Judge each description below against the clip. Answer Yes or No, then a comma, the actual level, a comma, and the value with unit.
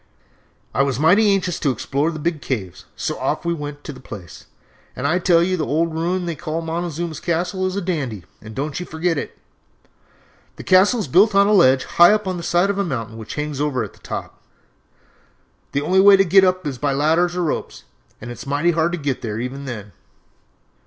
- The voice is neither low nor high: Yes, medium, 160 Hz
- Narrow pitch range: No, average, 4.6 semitones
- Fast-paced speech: Yes, fast, 220 wpm